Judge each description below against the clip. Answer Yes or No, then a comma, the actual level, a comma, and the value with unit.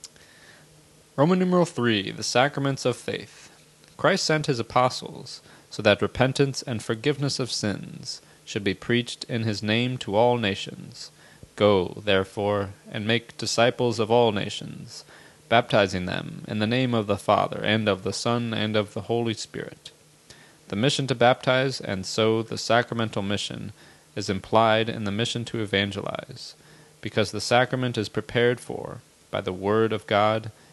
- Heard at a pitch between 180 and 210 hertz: No, low, 115 Hz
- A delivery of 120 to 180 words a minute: Yes, average, 155 wpm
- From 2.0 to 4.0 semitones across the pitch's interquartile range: Yes, average, 3.2 semitones